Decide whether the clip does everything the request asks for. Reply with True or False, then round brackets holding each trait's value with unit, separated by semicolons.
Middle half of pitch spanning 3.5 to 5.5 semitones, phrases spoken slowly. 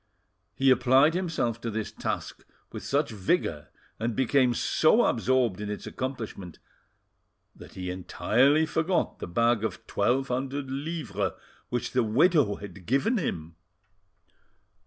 True (4.9 semitones; 130 wpm)